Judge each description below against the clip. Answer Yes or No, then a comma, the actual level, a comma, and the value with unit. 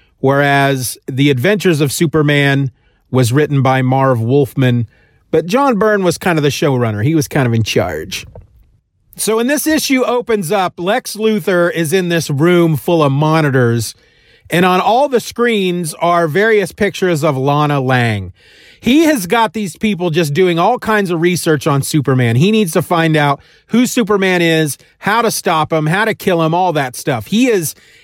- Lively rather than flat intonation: Yes, wide, 6.5 semitones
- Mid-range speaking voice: Yes, medium, 170 Hz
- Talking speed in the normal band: Yes, average, 180 wpm